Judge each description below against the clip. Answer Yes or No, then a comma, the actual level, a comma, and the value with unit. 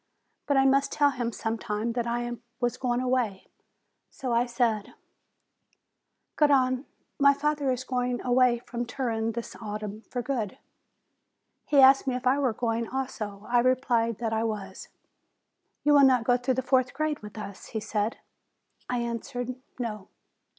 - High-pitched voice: Yes, high, 245 Hz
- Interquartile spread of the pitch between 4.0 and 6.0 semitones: No, narrow, 2.4 semitones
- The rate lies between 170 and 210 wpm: No, average, 155 wpm